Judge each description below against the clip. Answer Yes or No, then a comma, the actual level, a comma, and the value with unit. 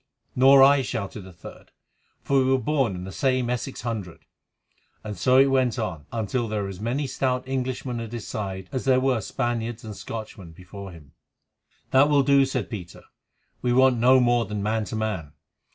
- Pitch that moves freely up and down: No, average, 4.2 semitones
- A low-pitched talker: Yes, low, 120 Hz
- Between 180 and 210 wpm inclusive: Yes, average, 190 wpm